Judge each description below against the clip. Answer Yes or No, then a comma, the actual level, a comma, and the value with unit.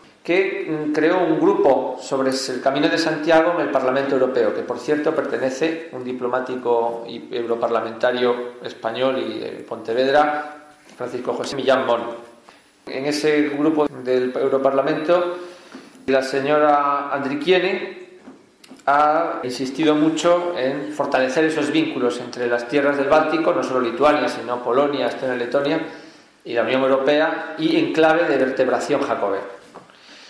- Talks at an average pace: Yes, average, 135 wpm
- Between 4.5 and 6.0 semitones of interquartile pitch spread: No, average, 3.7 semitones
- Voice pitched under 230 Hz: Yes, medium, 140 Hz